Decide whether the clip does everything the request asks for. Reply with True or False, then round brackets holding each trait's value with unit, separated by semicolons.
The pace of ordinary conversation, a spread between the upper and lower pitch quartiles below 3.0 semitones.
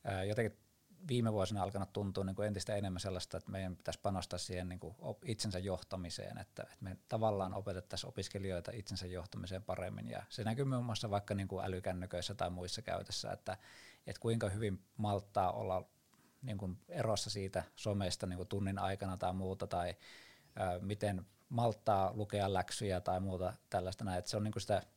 False (165 wpm; 2.4 semitones)